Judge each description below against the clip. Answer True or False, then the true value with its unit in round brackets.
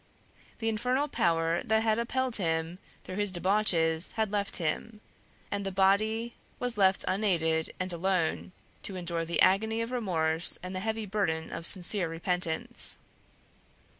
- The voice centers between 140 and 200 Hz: True (190 Hz)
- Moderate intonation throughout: True (4.4 semitones)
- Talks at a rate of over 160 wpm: False (145 wpm)